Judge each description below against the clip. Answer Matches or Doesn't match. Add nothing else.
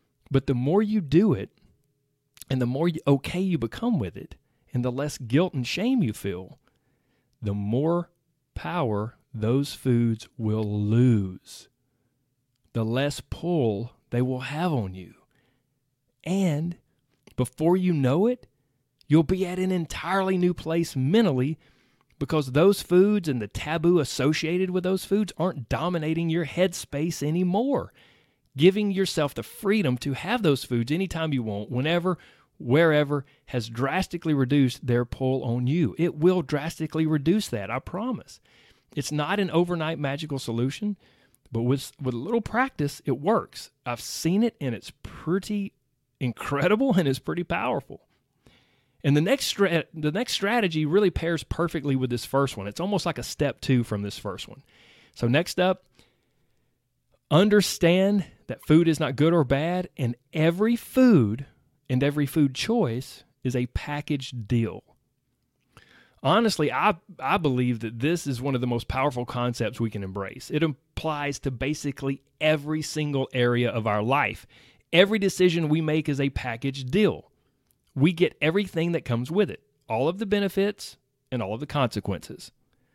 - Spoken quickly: Doesn't match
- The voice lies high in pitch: Doesn't match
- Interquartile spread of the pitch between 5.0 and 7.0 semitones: Matches